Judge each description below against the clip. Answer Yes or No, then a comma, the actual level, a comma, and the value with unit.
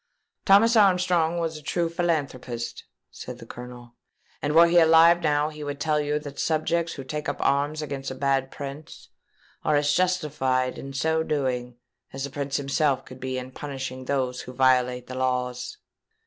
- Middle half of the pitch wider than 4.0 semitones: No, average, 3.6 semitones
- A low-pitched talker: No, medium, 145 Hz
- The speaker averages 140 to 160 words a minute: No, average, 175 wpm